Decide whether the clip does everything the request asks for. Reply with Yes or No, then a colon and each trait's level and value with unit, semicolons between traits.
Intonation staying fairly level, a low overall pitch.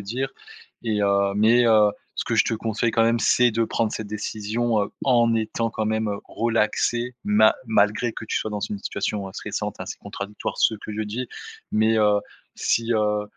Yes: narrow, 1.7 semitones; low, 110 Hz